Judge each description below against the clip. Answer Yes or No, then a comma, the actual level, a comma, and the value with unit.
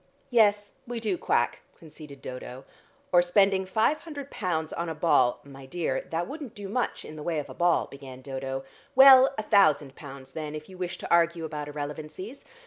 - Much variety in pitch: Yes, wide, 5.9 semitones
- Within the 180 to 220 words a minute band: Yes, average, 195 wpm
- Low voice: No, medium, 165 Hz